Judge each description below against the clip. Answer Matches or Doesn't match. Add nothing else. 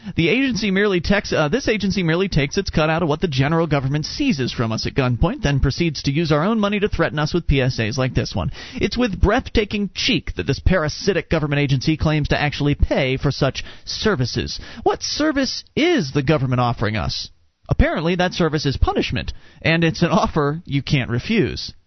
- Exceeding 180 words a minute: Matches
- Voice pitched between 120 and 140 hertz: Doesn't match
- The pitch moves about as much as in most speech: Doesn't match